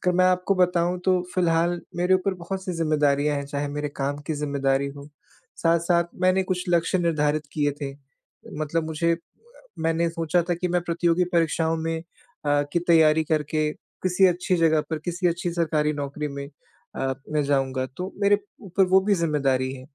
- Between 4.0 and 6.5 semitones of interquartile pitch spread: No, average, 3.2 semitones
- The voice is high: No, medium, 165 Hz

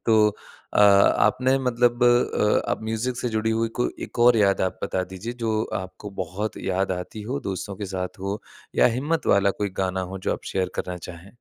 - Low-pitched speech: Yes, low, 105 Hz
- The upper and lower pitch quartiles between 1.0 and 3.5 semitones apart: No, average, 3.9 semitones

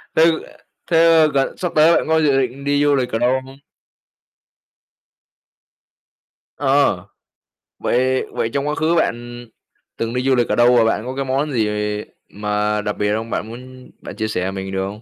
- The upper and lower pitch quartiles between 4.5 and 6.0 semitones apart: No, average, 4.1 semitones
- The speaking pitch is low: Yes, low, 130 Hz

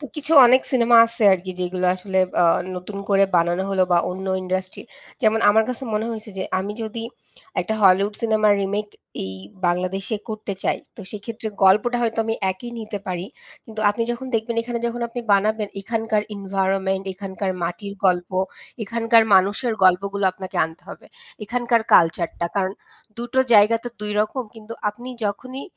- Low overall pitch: No, high, 205 Hz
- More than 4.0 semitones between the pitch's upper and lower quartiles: No, average, 3.2 semitones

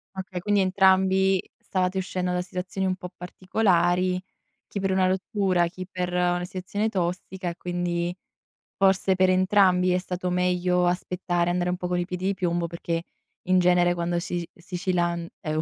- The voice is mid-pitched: Yes, medium, 180 Hz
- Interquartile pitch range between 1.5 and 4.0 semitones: No, narrow, 1.1 semitones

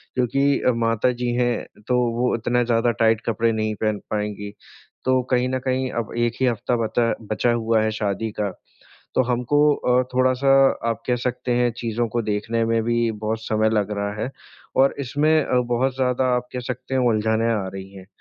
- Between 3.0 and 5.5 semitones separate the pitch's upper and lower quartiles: No, narrow, 2.4 semitones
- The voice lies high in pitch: No, low, 120 Hz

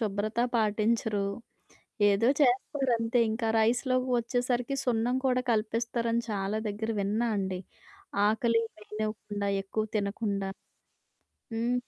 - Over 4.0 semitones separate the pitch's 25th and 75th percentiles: No, narrow, 2.4 semitones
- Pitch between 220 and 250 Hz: Yes, high, 225 Hz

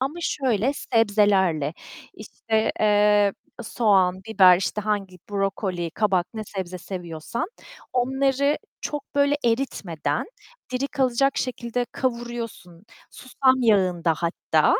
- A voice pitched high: Yes, high, 210 Hz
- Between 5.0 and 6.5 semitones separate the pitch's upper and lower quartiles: Yes, average, 5.3 semitones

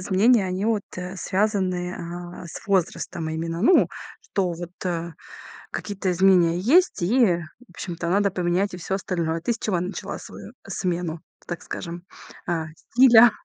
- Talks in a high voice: No, medium, 180 Hz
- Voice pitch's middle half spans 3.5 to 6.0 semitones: No, average, 2.7 semitones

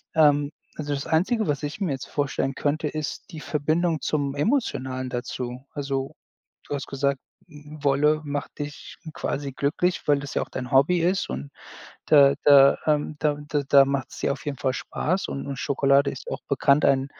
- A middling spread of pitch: No, narrow, 1.9 semitones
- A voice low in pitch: No, medium, 145 Hz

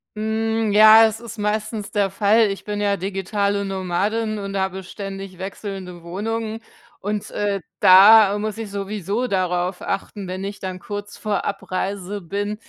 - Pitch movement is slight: Yes, narrow, 1.8 semitones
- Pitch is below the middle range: No, high, 200 Hz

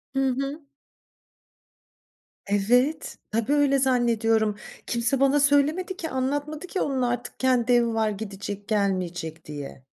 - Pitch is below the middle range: No, high, 245 Hz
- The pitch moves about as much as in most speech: Yes, average, 4.8 semitones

